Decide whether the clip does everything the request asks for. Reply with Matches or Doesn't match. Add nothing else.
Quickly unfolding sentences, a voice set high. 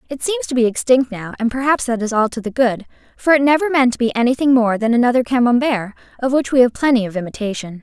Matches